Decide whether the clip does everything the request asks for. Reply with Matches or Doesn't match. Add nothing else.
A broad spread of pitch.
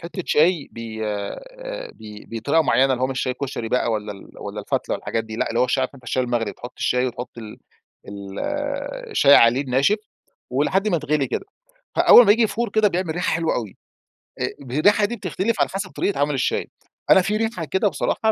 Matches